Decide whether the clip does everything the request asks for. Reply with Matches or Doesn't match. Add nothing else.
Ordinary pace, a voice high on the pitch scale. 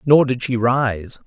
Doesn't match